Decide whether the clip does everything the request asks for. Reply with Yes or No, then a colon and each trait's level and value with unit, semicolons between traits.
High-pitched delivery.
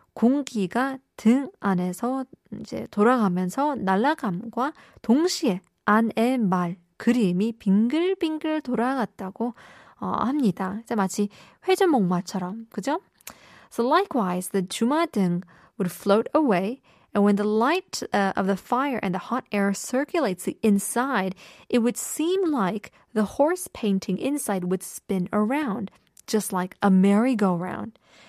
Yes: high, 215 Hz